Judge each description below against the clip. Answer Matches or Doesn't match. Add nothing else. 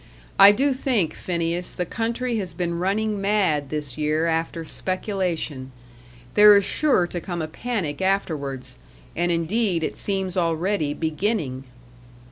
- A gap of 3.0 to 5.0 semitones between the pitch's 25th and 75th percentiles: Matches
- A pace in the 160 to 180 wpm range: Doesn't match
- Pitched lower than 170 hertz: Doesn't match